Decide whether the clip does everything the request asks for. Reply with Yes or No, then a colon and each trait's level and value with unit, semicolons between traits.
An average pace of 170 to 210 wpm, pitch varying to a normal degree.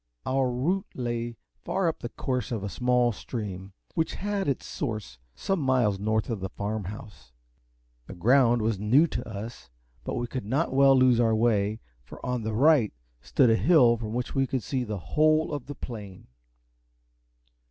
Yes: average, 180 wpm; average, 3.9 semitones